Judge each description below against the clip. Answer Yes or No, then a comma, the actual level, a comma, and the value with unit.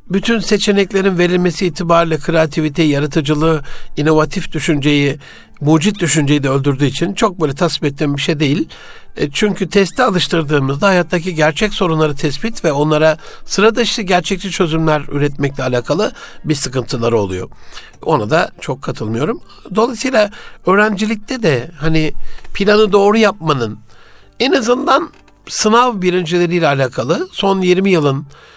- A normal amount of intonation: Yes, average, 5.0 semitones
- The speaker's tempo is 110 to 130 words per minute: Yes, average, 120 wpm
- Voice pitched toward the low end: No, medium, 170 Hz